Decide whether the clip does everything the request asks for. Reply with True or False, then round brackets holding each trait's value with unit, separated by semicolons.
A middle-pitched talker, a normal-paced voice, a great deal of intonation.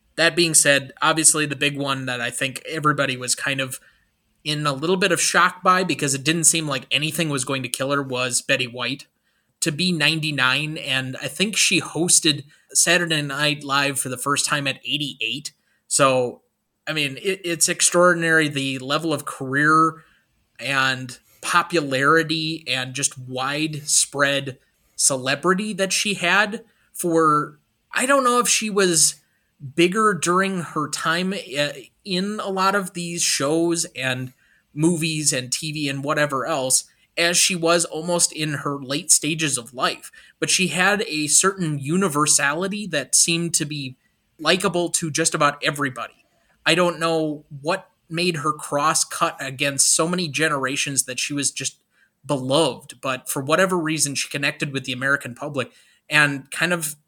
False (150 Hz; 160 wpm; 3.6 semitones)